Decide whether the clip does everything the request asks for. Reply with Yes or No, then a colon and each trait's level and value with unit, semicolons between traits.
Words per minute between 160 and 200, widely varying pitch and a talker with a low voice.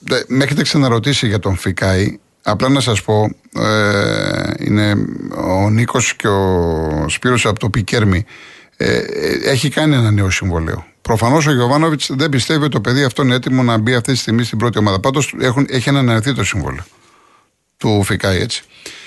No: fast, 170 wpm; average, 4.9 semitones; low, 115 Hz